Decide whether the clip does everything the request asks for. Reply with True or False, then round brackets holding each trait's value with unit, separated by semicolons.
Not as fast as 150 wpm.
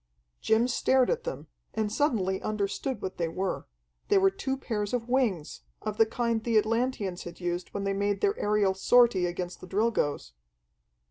False (175 wpm)